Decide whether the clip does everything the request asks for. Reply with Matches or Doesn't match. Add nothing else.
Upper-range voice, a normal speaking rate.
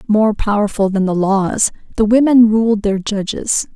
Matches